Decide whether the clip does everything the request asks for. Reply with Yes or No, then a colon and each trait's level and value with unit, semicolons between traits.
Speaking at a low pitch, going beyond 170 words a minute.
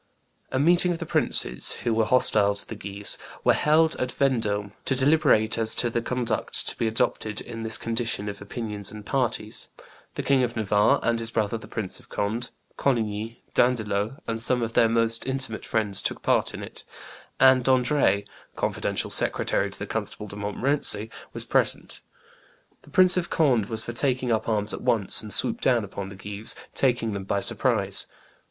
Yes: low, 115 Hz; average, 185 wpm